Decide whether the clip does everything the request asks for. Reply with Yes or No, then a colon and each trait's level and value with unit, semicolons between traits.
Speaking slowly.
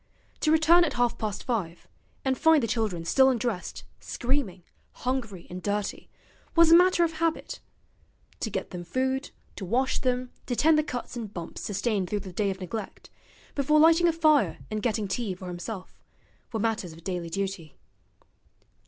No: average, 170 wpm